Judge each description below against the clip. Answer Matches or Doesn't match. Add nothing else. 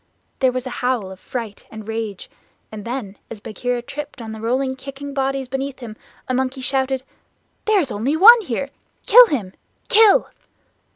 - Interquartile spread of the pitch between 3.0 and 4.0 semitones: Matches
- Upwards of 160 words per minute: Matches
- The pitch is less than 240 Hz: Doesn't match